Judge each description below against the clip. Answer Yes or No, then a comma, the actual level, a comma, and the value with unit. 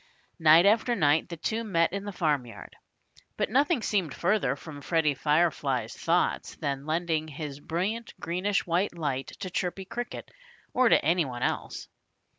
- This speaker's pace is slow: No, average, 155 wpm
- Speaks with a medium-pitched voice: Yes, medium, 170 Hz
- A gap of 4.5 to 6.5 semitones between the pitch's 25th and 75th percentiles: Yes, average, 5.0 semitones